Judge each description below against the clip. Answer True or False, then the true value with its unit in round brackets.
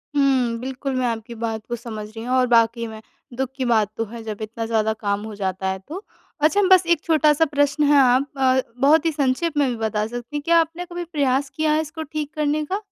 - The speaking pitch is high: True (260 Hz)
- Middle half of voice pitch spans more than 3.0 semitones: True (5.1 semitones)